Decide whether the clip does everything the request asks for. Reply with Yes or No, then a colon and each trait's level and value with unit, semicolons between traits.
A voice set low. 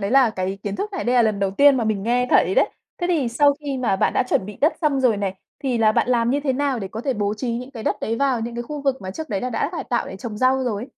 No: high, 245 Hz